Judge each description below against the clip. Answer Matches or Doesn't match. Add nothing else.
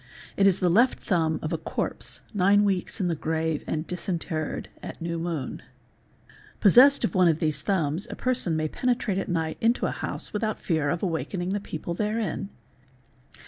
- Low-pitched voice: Doesn't match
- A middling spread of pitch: Matches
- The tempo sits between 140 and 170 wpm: Doesn't match